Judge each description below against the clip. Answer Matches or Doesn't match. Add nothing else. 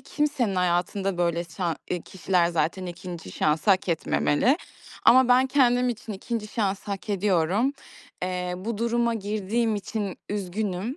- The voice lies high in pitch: Matches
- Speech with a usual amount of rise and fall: Matches